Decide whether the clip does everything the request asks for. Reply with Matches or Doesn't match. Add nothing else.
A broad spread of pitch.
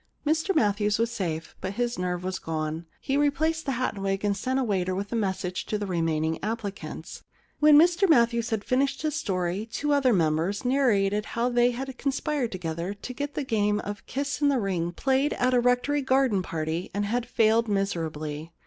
Matches